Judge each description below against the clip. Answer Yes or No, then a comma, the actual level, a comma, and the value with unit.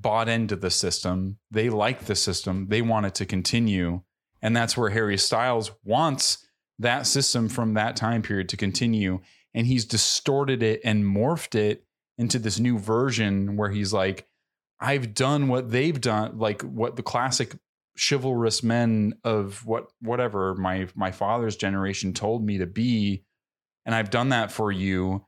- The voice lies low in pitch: Yes, low, 110 Hz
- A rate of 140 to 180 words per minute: Yes, average, 165 wpm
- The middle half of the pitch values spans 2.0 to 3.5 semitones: Yes, average, 3.1 semitones